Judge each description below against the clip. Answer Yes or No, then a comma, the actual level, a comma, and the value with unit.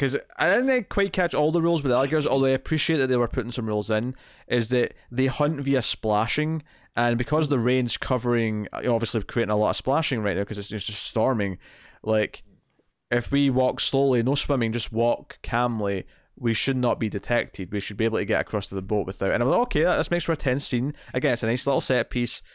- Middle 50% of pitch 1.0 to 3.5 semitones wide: No, average, 3.9 semitones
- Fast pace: Yes, fast, 235 wpm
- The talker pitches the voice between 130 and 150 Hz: No, low, 120 Hz